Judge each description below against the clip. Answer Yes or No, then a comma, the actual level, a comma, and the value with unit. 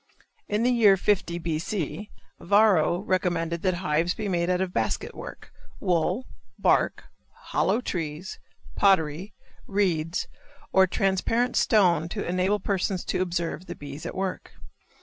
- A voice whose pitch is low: No, medium, 185 Hz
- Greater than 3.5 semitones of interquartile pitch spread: No, average, 3.0 semitones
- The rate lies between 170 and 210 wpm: No, slow, 135 wpm